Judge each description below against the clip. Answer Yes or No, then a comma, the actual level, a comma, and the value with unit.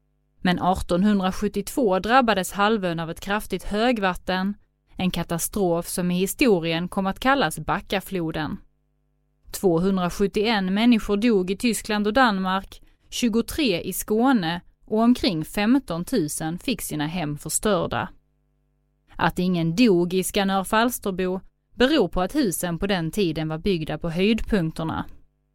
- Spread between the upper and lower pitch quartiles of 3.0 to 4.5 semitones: Yes, average, 3.6 semitones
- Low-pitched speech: No, high, 190 Hz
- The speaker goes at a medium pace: No, slow, 120 wpm